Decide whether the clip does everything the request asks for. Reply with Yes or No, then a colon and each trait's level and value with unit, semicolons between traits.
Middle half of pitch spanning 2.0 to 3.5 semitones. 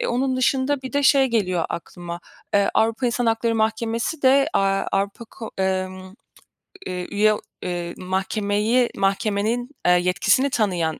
No: average, 4.6 semitones